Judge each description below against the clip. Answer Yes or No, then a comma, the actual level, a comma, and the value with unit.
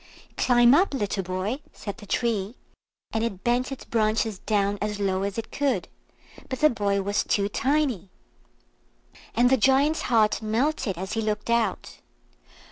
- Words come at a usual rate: Yes, average, 155 wpm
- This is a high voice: Yes, high, 220 Hz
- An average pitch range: Yes, average, 3.8 semitones